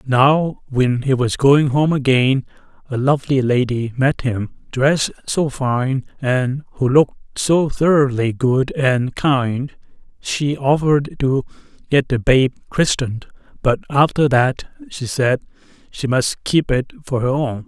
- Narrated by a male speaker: Yes, male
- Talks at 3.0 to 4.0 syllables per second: Yes, 3.9 syllables/s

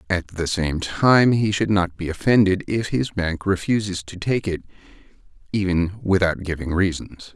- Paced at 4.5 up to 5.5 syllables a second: Yes, 4.6 syllables/s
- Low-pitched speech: Yes, very low, 95 Hz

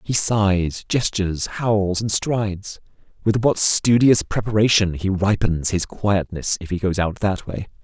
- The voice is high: No, low, 100 Hz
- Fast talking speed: No, average, 155 wpm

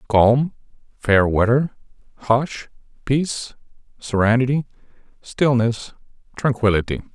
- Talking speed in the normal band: No, slow, 65 wpm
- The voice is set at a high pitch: No, low, 120 Hz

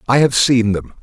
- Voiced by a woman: No, male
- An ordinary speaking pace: No, fast, 235 wpm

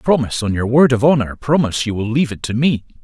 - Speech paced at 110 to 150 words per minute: No, fast, 220 wpm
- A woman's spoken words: No, male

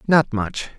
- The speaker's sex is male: Yes, male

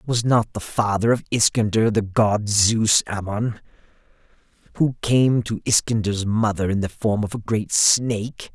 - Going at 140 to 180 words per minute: Yes, average, 155 wpm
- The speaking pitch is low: Yes, low, 110 Hz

